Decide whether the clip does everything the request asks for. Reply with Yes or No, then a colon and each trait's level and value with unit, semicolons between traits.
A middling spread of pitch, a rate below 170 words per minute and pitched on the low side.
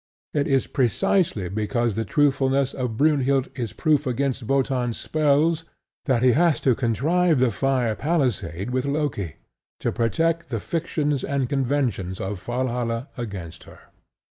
Yes: average, 3.9 semitones; average, 140 wpm; low, 130 Hz